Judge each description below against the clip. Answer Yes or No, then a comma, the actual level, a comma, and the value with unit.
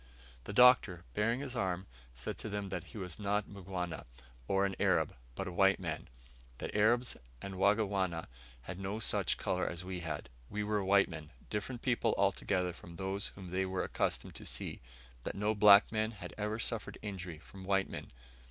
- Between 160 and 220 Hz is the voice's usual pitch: No, low, 100 Hz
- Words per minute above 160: Yes, average, 190 wpm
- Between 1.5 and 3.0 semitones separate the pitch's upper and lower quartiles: Yes, narrow, 2.4 semitones